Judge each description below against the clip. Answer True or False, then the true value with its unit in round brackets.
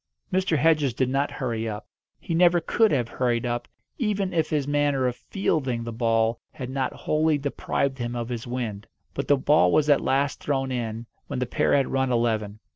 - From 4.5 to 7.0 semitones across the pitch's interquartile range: False (3.8 semitones)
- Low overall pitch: True (130 Hz)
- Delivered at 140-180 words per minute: False (200 wpm)